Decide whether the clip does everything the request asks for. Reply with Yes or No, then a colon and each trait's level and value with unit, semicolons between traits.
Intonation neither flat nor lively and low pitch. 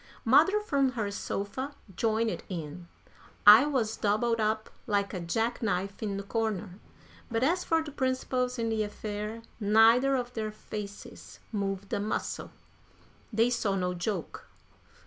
No: average, 3.5 semitones; high, 220 Hz